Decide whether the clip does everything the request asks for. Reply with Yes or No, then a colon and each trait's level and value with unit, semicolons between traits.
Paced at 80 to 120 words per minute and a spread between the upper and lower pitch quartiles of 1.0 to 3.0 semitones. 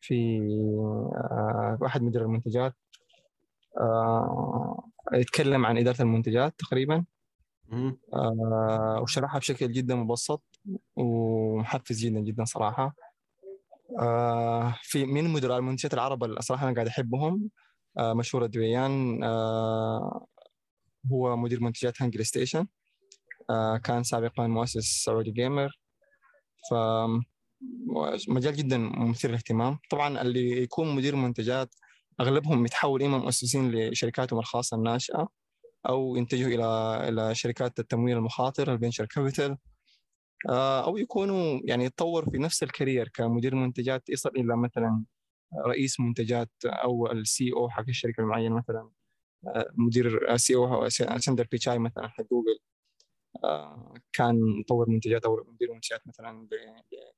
Yes: average, 110 wpm; average, 2.7 semitones